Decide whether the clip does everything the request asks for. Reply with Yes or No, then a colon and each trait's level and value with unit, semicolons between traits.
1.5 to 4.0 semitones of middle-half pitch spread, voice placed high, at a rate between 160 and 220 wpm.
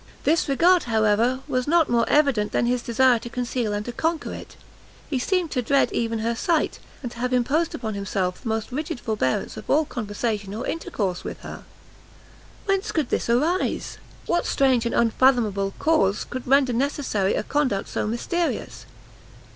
No: average, 4.7 semitones; high, 245 Hz; average, 170 wpm